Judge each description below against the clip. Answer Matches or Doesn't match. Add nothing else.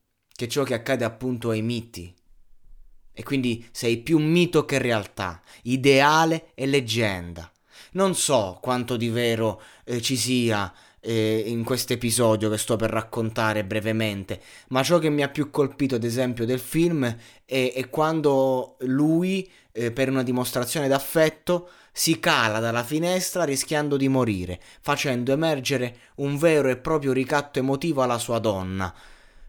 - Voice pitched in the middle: Doesn't match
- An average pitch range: Matches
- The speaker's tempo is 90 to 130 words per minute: Doesn't match